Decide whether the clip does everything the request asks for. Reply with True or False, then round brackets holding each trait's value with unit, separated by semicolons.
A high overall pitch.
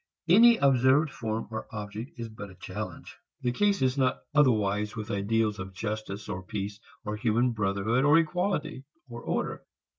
False (115 Hz)